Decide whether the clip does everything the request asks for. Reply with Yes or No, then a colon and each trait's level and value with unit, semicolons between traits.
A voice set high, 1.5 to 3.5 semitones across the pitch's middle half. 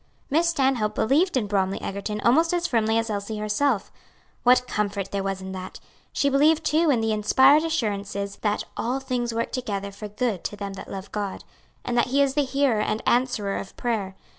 No: high, 225 Hz; average, 5.0 semitones